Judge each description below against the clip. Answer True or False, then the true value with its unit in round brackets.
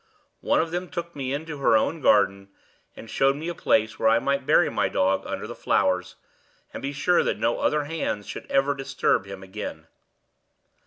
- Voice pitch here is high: False (135 Hz)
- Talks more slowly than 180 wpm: False (195 wpm)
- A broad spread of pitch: True (6.7 semitones)